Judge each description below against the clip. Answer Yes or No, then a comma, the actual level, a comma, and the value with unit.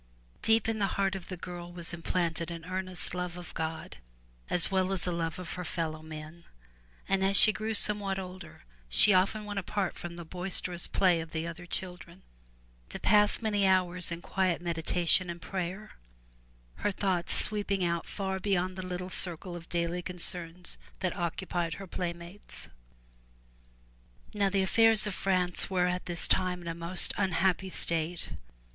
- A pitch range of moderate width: No, narrow, 2.0 semitones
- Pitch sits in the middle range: Yes, medium, 180 Hz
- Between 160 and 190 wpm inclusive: Yes, average, 165 wpm